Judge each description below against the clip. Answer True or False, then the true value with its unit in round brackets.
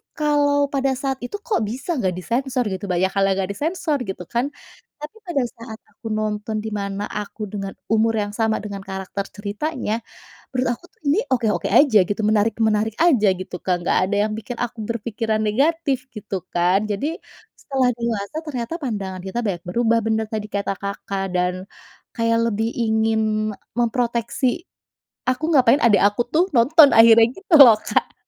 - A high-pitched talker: True (225 Hz)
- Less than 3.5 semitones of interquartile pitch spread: False (4.0 semitones)